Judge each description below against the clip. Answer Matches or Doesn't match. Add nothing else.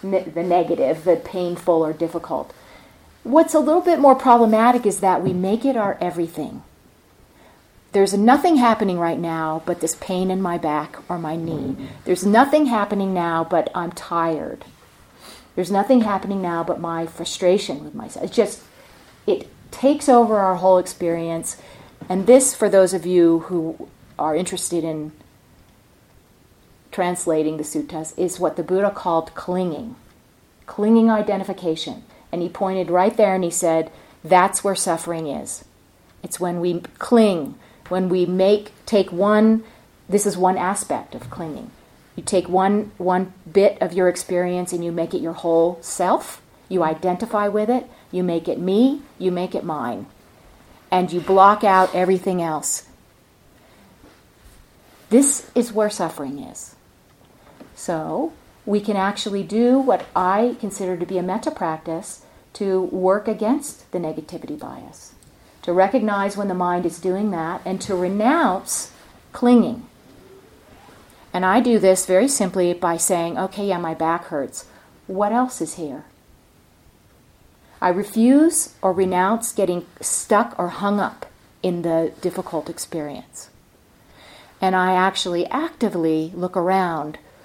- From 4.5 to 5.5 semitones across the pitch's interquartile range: Doesn't match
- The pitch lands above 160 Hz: Matches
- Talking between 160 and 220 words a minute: Doesn't match